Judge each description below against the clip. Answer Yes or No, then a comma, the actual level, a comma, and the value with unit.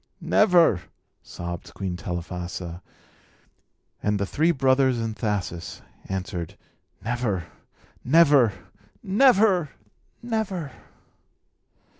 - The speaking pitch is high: No, low, 115 Hz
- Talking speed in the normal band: No, slow, 75 wpm